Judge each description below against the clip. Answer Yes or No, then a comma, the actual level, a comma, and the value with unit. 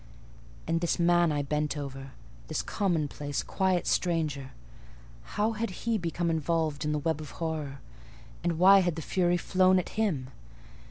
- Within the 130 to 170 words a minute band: Yes, average, 145 wpm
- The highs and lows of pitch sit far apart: No, average, 3.5 semitones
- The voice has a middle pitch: Yes, medium, 160 Hz